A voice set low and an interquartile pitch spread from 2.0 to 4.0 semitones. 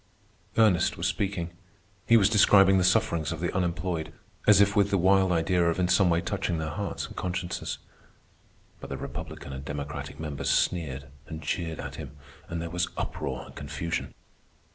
Yes: very low, 85 Hz; average, 3.1 semitones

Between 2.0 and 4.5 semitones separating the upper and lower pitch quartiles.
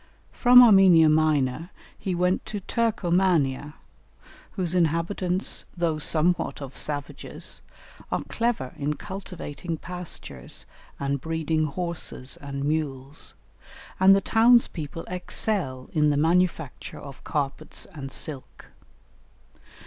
Yes: average, 3.9 semitones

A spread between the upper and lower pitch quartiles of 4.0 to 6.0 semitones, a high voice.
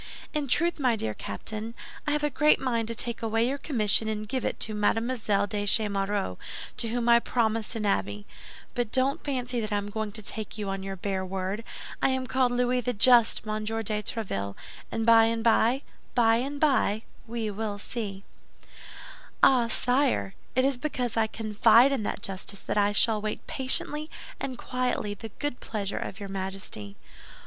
No: average, 3.3 semitones; high, 225 Hz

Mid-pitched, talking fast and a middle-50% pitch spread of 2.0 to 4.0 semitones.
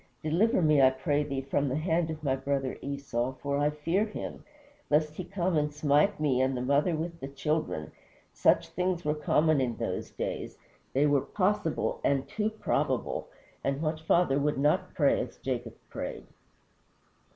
No: medium, 150 Hz; average, 175 wpm; average, 3.0 semitones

